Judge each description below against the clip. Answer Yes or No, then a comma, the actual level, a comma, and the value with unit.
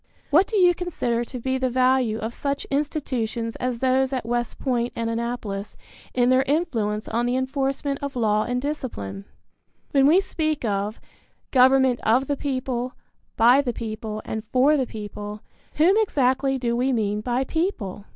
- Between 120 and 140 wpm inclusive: No, average, 165 wpm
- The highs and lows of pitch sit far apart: No, average, 3.2 semitones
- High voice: Yes, very high, 250 Hz